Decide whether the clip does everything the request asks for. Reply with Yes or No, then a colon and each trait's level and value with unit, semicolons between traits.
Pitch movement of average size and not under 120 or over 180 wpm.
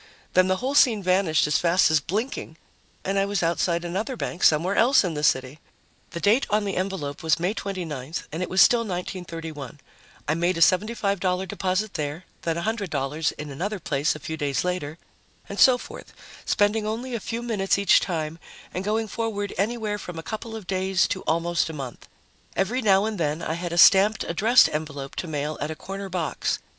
No: average, 4.4 semitones; average, 195 wpm